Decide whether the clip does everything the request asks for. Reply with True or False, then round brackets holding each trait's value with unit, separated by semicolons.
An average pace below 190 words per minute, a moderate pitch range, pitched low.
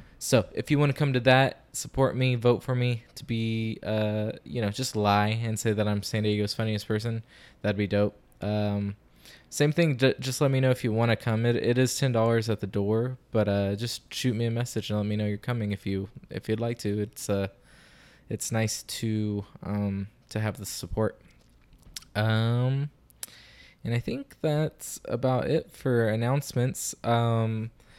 False (195 wpm; 3.2 semitones; 115 Hz)